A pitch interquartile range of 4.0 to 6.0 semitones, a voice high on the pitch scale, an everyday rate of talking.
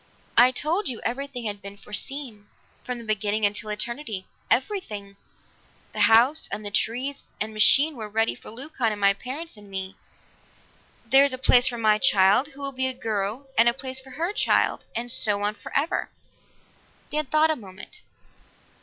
Yes: average, 4.5 semitones; high, 235 Hz; average, 170 wpm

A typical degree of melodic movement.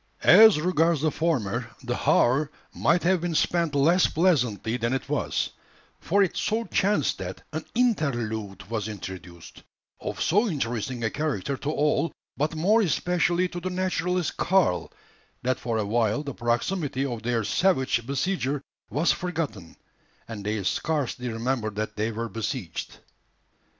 No: wide, 7.1 semitones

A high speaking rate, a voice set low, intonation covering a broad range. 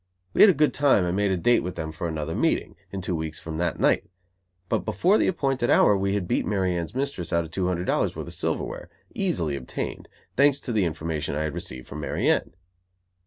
Yes: fast, 230 wpm; very low, 90 Hz; wide, 6.9 semitones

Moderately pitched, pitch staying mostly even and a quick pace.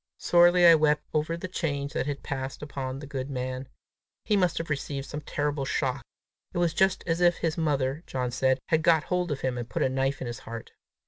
No: medium, 145 Hz; average, 3.9 semitones; fast, 220 wpm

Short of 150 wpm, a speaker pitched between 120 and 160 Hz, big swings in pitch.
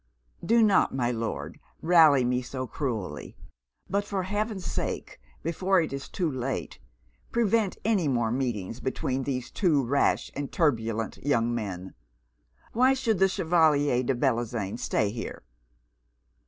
Yes: slow, 135 wpm; medium, 140 Hz; wide, 7.5 semitones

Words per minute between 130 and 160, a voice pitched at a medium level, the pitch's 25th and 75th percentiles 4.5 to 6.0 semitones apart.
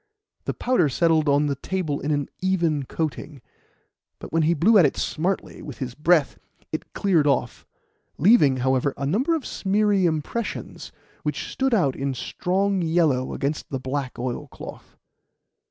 Yes: average, 155 wpm; medium, 155 Hz; average, 5.3 semitones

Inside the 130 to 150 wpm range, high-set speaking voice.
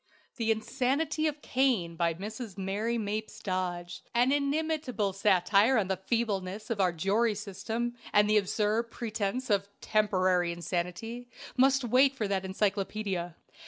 Yes: slow, 135 wpm; high, 210 Hz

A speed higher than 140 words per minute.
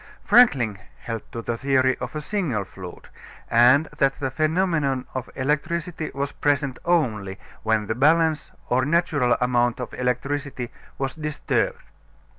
No: slow, 135 wpm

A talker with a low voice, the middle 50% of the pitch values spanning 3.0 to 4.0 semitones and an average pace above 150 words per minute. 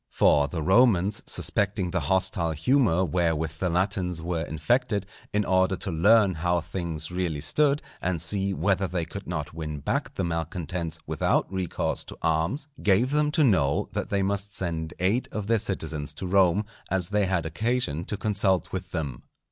Yes: very low, 90 Hz; average, 3.7 semitones; average, 170 wpm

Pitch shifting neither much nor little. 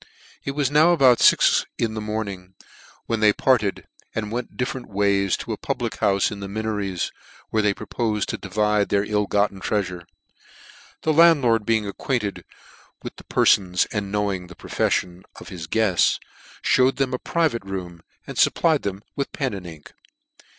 Yes: average, 3.7 semitones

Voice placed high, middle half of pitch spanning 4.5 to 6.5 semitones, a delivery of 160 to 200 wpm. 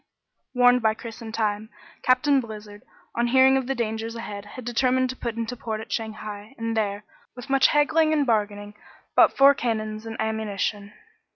No: high, 225 Hz; average, 3.0 semitones; average, 175 wpm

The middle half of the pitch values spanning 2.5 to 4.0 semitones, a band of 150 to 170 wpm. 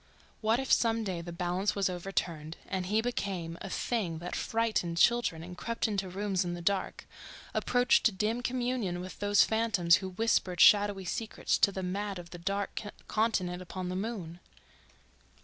Yes: average, 3.7 semitones; average, 165 wpm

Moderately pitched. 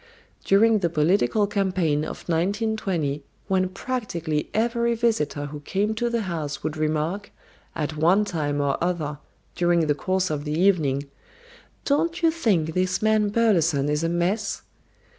Yes: medium, 180 Hz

